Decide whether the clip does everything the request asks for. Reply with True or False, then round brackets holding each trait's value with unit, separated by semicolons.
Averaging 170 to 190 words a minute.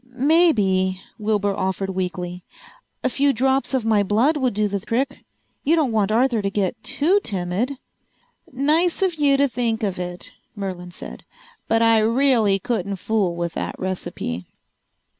False (155 wpm)